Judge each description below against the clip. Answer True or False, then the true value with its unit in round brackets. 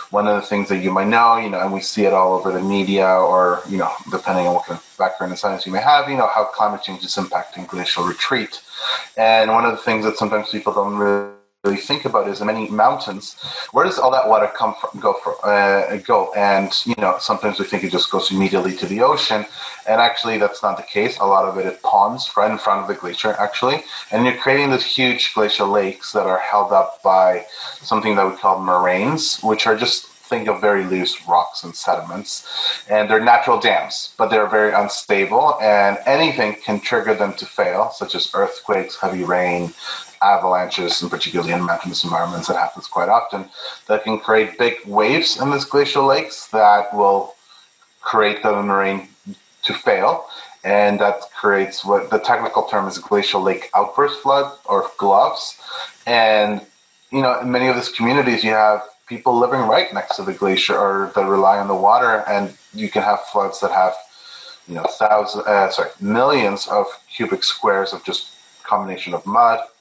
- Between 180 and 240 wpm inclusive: True (200 wpm)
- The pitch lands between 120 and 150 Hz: False (105 Hz)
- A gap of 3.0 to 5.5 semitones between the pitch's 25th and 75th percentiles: False (2.4 semitones)